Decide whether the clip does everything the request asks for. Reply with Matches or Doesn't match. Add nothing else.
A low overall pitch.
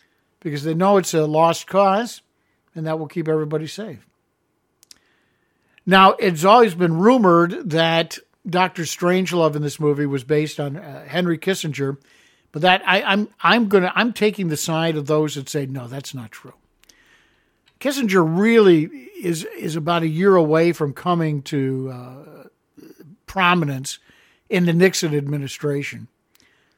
Doesn't match